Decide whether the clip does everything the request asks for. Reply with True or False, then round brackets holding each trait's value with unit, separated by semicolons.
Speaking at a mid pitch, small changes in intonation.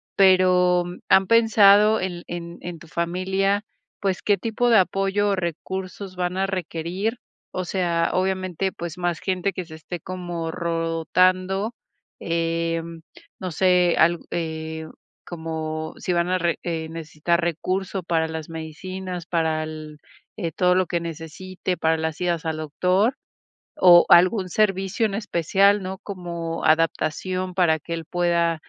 True (175 Hz; 2.3 semitones)